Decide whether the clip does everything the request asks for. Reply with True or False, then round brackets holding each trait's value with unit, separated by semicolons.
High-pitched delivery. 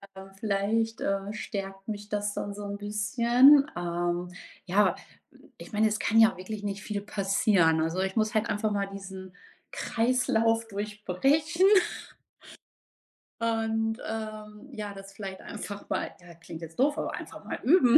True (210 Hz)